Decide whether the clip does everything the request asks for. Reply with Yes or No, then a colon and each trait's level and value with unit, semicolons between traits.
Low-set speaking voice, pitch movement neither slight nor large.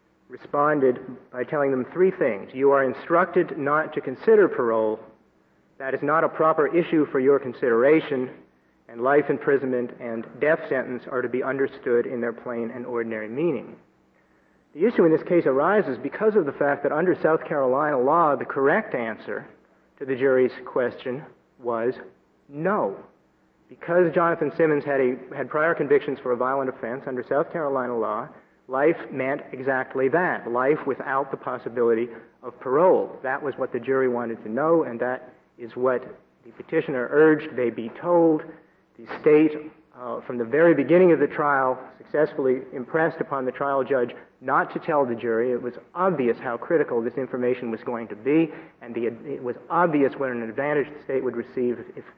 Yes: low, 130 Hz; average, 4.0 semitones